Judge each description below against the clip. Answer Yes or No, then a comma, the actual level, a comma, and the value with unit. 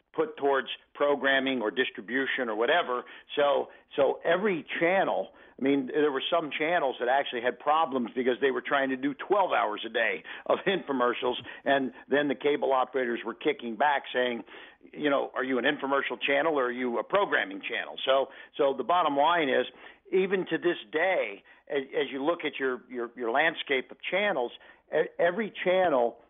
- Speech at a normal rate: Yes, average, 180 wpm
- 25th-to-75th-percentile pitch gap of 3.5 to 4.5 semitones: No, average, 2.9 semitones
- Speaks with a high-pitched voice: No, low, 135 Hz